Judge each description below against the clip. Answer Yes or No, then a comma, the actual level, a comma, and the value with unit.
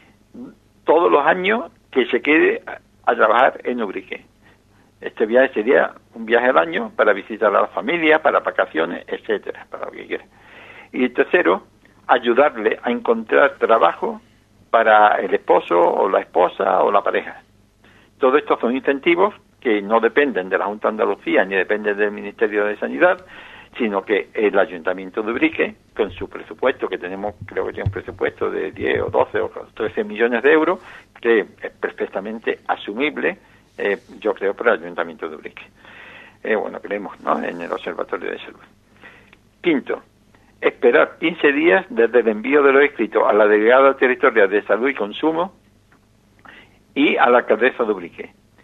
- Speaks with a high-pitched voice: Yes, high, 240 Hz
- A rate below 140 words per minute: No, average, 165 wpm